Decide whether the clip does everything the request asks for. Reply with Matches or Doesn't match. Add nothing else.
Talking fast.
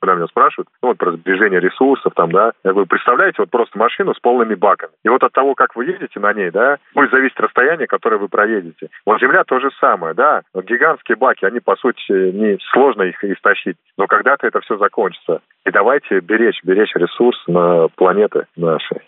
Matches